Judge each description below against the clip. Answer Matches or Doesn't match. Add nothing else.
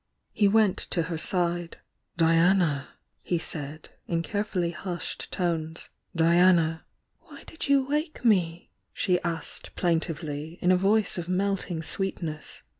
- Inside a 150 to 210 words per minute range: Doesn't match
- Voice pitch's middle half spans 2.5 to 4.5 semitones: Matches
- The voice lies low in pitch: Doesn't match